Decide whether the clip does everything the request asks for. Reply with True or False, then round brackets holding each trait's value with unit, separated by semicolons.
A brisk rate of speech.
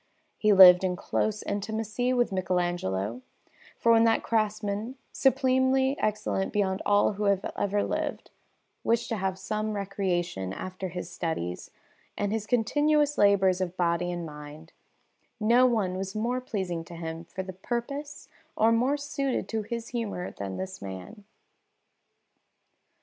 False (140 wpm)